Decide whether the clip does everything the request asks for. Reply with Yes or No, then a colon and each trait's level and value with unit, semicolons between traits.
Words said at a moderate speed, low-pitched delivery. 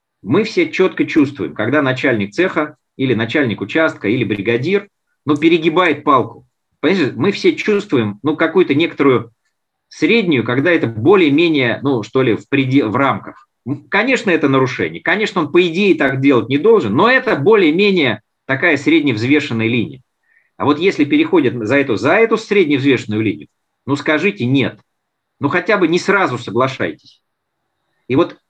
No: average, 150 wpm; medium, 155 Hz